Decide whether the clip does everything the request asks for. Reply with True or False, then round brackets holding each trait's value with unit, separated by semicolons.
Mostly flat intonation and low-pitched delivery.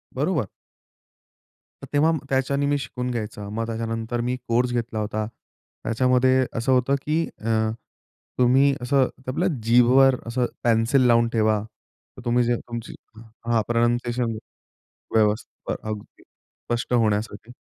True (2.1 semitones; 120 Hz)